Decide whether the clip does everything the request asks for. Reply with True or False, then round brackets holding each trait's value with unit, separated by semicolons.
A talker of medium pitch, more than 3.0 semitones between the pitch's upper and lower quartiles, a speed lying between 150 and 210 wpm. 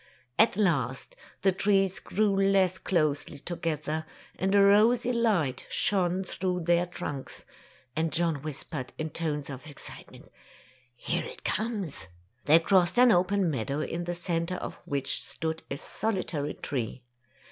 False (175 Hz; 4.4 semitones; 140 wpm)